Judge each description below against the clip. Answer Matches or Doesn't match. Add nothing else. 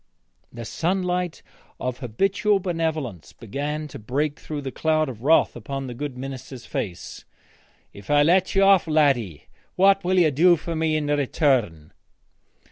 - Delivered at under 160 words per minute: Matches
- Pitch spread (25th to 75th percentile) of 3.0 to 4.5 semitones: Doesn't match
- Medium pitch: Matches